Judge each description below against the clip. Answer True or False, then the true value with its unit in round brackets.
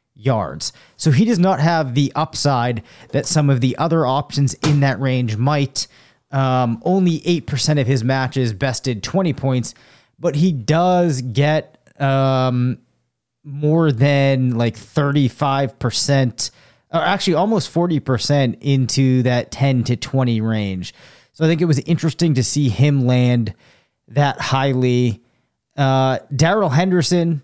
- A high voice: False (135 Hz)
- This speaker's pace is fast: False (135 wpm)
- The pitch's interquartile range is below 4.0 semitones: True (3.5 semitones)